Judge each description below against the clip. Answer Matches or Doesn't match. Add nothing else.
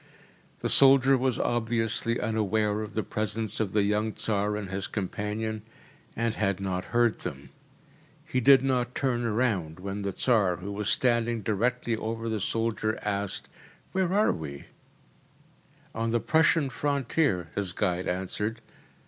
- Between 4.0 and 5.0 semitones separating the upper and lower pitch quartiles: Doesn't match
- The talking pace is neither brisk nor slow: Matches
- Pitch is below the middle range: Matches